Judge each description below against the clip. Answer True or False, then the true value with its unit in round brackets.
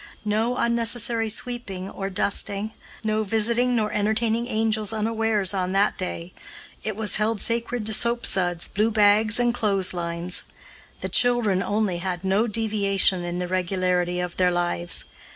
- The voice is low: False (210 Hz)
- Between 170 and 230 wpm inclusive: False (145 wpm)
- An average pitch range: True (3.3 semitones)